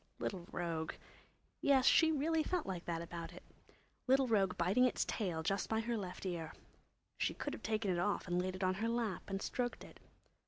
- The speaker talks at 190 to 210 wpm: Yes, average, 200 wpm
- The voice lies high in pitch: Yes, high, 195 Hz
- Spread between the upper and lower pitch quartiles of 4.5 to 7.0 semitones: Yes, average, 5.3 semitones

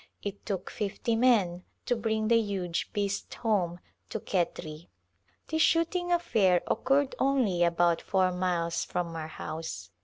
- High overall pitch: Yes, high, 195 Hz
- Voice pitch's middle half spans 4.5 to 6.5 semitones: Yes, average, 4.9 semitones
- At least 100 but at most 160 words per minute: Yes, slow, 135 wpm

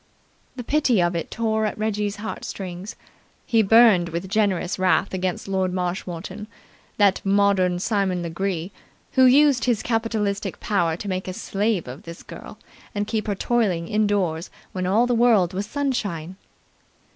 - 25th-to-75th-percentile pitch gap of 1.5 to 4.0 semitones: Yes, average, 3.3 semitones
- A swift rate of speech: No, average, 155 wpm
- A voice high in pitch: Yes, high, 200 Hz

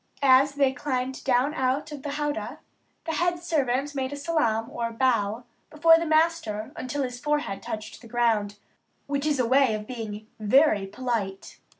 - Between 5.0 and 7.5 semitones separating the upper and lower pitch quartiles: No, average, 4.5 semitones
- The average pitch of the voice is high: Yes, very high, 260 Hz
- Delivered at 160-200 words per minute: Yes, average, 170 wpm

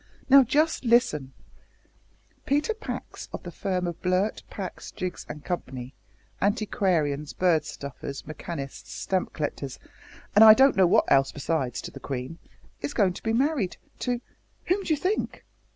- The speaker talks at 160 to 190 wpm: No, average, 150 wpm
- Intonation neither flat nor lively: No, wide, 8.1 semitones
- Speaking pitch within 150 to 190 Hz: Yes, medium, 185 Hz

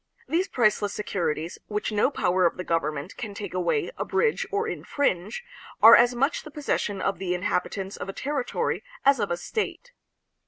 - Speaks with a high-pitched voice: Yes, high, 205 Hz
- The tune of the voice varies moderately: No, wide, 7.2 semitones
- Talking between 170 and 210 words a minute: Yes, average, 180 wpm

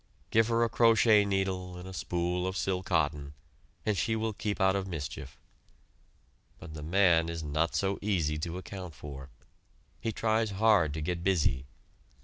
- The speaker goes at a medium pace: Yes, average, 165 wpm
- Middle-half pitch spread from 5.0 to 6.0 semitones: No, average, 4.0 semitones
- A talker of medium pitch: No, very low, 90 Hz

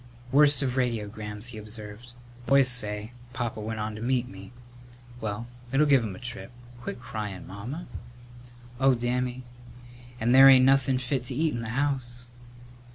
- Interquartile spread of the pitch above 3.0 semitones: Yes, average, 3.4 semitones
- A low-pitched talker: Yes, low, 120 Hz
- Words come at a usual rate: Yes, average, 160 wpm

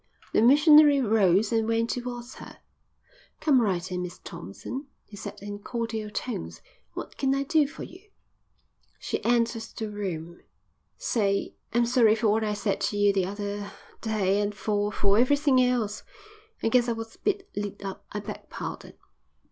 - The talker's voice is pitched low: No, high, 220 Hz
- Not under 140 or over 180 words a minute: Yes, average, 170 wpm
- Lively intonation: No, average, 3.4 semitones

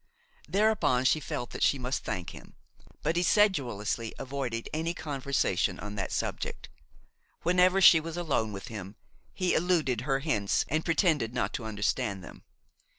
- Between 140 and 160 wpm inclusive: Yes, average, 150 wpm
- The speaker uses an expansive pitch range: Yes, wide, 6.7 semitones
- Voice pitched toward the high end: No, low, 135 Hz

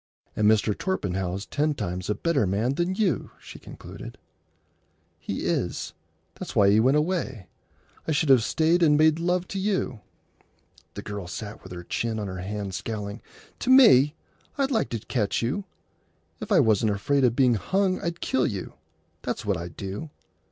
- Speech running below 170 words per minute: No, average, 175 wpm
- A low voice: Yes, low, 120 Hz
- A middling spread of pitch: No, wide, 8.5 semitones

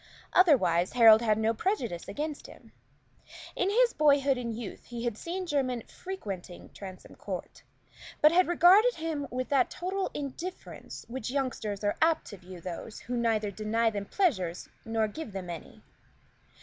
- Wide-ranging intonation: Yes, wide, 7.0 semitones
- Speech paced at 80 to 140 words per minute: No, average, 160 wpm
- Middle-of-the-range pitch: No, high, 245 Hz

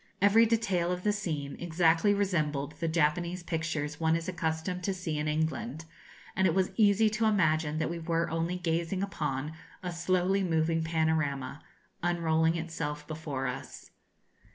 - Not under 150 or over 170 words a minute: Yes, average, 155 wpm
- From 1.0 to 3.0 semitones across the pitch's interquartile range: Yes, narrow, 2.5 semitones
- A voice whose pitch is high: No, medium, 165 Hz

